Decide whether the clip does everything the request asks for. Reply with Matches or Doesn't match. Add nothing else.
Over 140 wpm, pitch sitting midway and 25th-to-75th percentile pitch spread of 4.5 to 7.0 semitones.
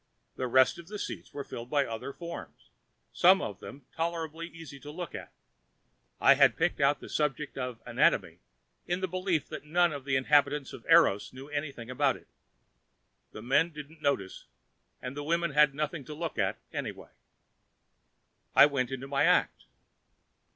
Doesn't match